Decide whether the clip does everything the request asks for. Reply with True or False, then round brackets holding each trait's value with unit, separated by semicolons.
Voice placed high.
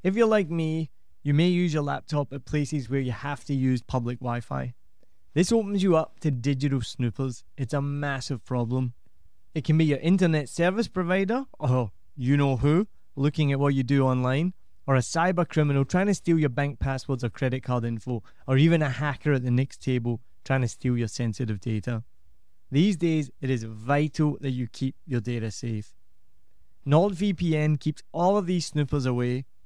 False (140 Hz)